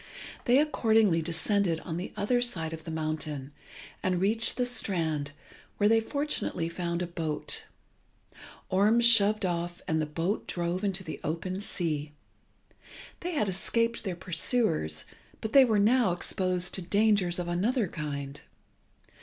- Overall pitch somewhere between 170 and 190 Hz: Yes, medium, 185 Hz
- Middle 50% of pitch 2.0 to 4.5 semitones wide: No, average, 5.0 semitones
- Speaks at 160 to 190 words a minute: No, average, 145 wpm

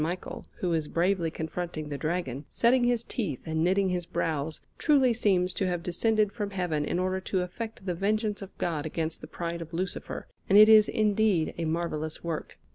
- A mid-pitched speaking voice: Yes, medium, 180 Hz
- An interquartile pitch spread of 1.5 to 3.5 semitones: No, average, 4.1 semitones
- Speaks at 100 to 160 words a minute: No, average, 195 wpm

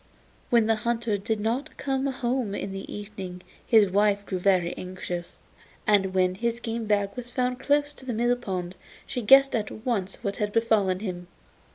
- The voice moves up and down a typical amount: Yes, average, 3.9 semitones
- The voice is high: Yes, high, 215 Hz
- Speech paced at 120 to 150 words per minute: No, average, 180 wpm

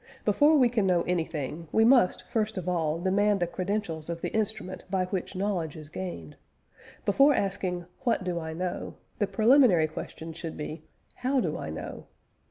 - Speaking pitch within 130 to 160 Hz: No, medium, 185 Hz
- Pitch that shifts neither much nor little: Yes, average, 4.3 semitones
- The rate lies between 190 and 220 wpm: No, average, 175 wpm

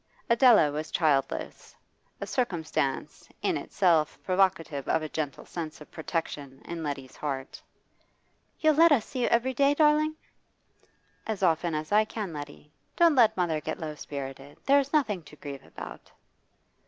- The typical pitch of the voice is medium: Yes, medium, 165 Hz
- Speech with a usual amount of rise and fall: No, wide, 7.9 semitones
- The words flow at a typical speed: Yes, average, 150 wpm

